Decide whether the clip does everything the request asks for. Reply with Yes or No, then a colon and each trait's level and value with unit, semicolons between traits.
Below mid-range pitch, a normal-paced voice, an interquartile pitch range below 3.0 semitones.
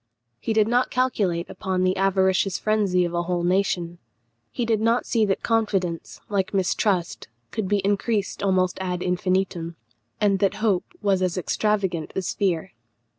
No: high, 190 Hz; average, 155 wpm; narrow, 2.6 semitones